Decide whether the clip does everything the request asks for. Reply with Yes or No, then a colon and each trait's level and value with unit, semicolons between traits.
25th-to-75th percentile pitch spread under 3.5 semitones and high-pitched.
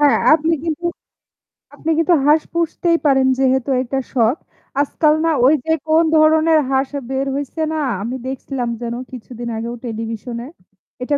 No: average, 4.5 semitones; very high, 270 Hz